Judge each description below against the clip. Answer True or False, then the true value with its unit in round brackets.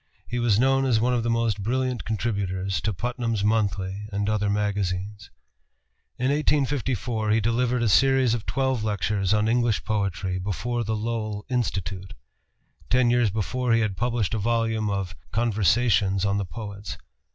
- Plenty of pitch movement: False (3.1 semitones)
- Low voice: True (110 Hz)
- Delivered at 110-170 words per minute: True (155 wpm)